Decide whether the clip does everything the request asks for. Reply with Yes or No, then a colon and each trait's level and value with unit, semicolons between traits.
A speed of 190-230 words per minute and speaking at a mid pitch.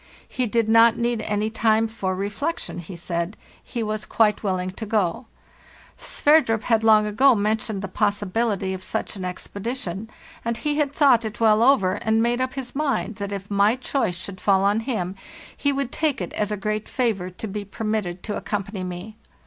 No: average, 195 wpm; high, 215 Hz